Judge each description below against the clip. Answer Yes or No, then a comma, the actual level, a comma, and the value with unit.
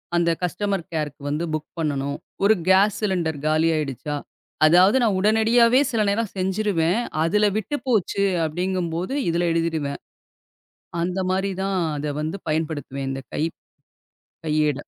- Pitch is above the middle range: No, medium, 175 Hz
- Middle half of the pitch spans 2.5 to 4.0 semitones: No, average, 4.4 semitones